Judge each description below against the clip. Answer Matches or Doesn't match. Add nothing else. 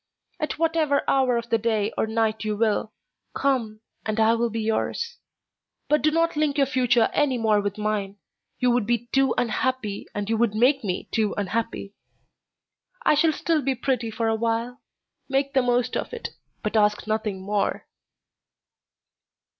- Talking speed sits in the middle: Matches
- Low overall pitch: Doesn't match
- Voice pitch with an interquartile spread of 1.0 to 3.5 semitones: Doesn't match